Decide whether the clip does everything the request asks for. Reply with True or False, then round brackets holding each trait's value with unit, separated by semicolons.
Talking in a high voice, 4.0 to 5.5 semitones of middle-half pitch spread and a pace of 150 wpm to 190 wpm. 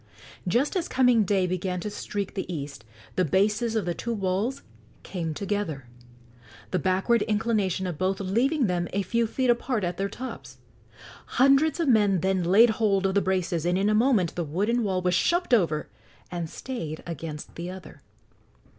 True (195 Hz; 4.6 semitones; 175 wpm)